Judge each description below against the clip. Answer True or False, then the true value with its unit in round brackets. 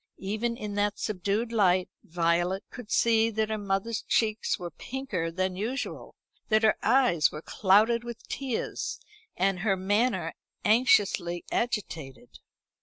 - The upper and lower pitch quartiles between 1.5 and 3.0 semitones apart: False (3.8 semitones)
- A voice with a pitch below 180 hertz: False (205 Hz)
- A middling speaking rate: False (130 wpm)